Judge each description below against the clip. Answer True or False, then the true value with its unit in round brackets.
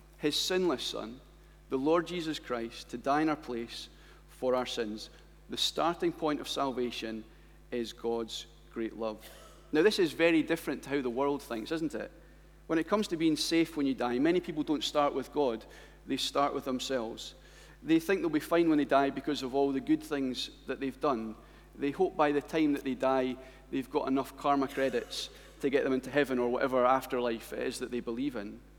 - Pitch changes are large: False (4.0 semitones)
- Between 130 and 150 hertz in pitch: True (140 Hz)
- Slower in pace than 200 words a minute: False (205 wpm)